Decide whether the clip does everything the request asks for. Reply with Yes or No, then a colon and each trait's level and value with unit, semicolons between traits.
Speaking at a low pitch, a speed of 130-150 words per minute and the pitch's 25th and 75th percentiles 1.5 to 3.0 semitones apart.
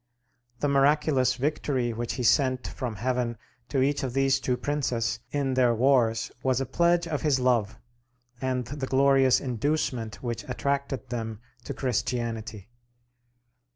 Yes: low, 130 Hz; average, 140 wpm; narrow, 2.6 semitones